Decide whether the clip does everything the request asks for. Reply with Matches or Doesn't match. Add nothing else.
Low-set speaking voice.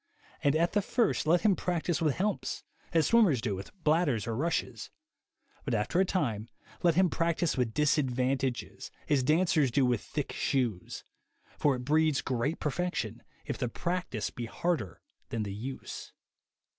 Doesn't match